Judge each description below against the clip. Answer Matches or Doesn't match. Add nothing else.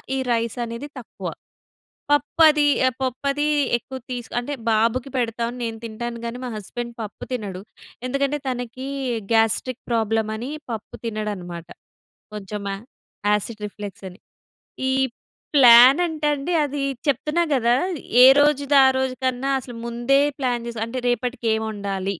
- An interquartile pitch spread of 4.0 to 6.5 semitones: Doesn't match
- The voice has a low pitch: Doesn't match